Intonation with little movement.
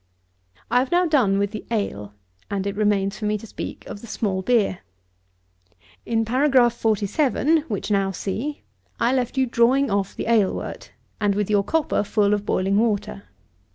No: average, 3.6 semitones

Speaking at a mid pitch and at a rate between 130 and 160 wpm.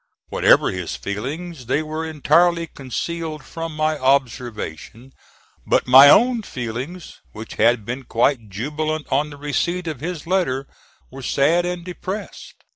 Yes: medium, 145 Hz; slow, 135 wpm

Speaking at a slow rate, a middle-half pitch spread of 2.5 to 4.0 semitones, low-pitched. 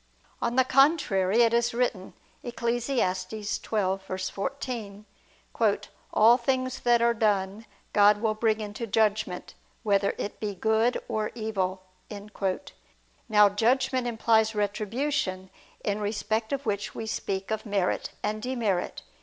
No: slow, 120 wpm; average, 2.8 semitones; high, 220 Hz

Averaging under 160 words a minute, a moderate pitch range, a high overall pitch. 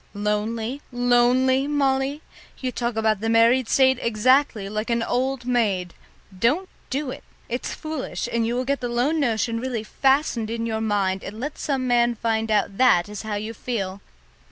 No: average, 175 wpm; average, 3.0 semitones; high, 235 Hz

